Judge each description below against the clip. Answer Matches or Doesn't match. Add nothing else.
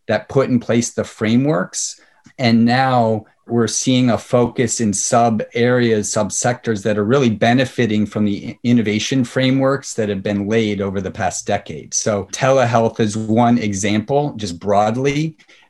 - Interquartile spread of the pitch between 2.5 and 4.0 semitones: Matches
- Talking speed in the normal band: Matches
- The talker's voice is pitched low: Matches